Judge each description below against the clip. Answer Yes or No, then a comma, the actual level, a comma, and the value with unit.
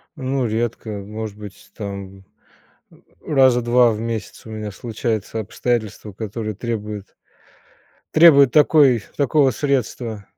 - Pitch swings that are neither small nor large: Yes, average, 3.2 semitones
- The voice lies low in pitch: Yes, low, 115 Hz